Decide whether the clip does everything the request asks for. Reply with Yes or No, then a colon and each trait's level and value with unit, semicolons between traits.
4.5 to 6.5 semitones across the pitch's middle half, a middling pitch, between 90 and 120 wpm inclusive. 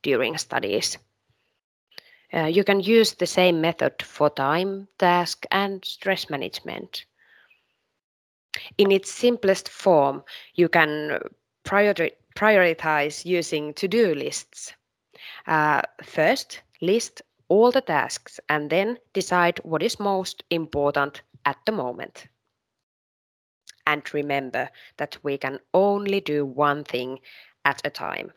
Yes: average, 5.0 semitones; medium, 175 Hz; average, 115 wpm